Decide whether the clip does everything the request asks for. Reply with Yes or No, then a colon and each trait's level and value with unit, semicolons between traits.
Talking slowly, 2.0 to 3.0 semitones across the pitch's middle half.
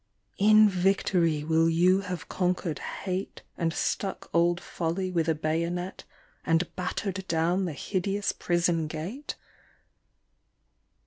Yes: slow, 115 wpm; narrow, 2.6 semitones